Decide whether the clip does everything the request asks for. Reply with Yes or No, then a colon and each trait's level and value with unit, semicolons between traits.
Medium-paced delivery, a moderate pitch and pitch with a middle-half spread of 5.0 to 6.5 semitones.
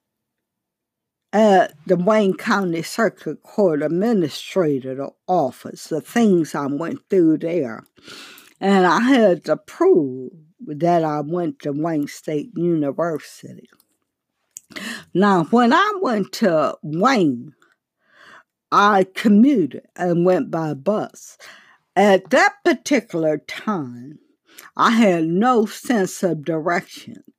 No: slow, 105 wpm; medium, 180 Hz; wide, 5.5 semitones